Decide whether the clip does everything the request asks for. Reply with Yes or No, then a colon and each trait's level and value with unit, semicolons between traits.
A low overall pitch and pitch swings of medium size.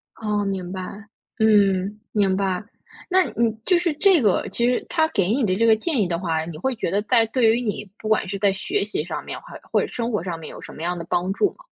No: high, 210 Hz; average, 4.2 semitones